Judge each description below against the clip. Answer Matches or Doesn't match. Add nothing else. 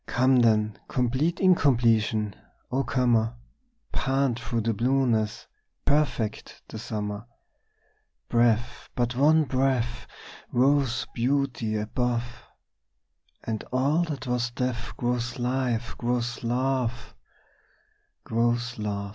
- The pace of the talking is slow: Matches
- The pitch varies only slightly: Matches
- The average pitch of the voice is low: Matches